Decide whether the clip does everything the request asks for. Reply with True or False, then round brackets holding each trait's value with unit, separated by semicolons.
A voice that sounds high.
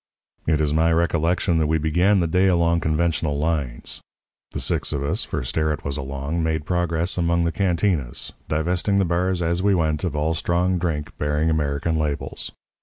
False (80 Hz)